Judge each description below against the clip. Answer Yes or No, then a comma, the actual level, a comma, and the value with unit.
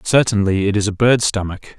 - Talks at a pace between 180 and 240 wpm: Yes, average, 200 wpm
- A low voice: Yes, low, 105 Hz